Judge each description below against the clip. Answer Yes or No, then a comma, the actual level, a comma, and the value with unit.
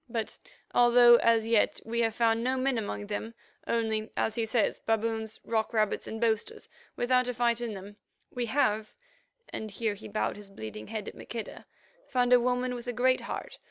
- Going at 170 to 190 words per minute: Yes, average, 180 wpm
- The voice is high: Yes, high, 230 Hz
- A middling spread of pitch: No, narrow, 2.1 semitones